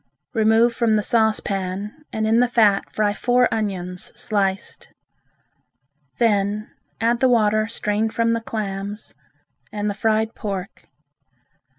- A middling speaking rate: No, slow, 120 wpm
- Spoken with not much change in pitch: Yes, narrow, 2.0 semitones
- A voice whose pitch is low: No, high, 215 Hz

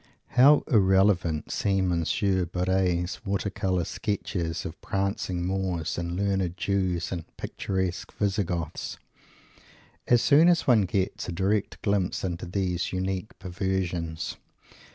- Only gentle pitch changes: Yes, narrow, 2.1 semitones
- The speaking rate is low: Yes, slow, 120 wpm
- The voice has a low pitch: Yes, very low, 95 Hz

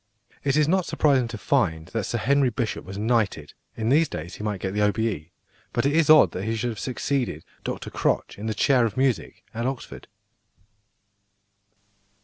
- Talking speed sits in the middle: Yes, average, 185 wpm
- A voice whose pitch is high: No, low, 115 Hz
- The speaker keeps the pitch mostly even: No, average, 4.8 semitones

